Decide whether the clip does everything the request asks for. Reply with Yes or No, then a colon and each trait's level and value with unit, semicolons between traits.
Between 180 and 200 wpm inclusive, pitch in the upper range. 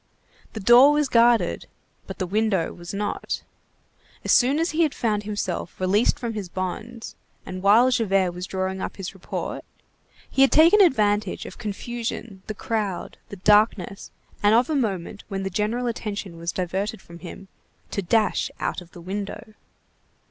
No: average, 165 wpm; high, 210 Hz